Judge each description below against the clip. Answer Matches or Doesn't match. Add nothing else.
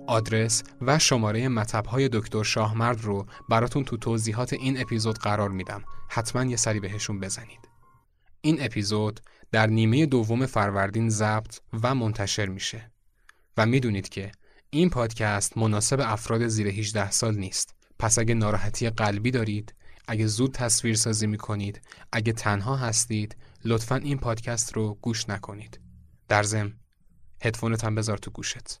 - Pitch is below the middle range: Matches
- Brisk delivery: Doesn't match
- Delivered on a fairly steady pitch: Matches